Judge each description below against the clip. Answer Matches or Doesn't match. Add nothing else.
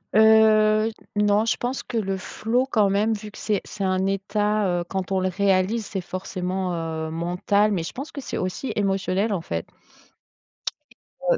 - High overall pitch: Matches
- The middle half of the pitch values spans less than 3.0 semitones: Matches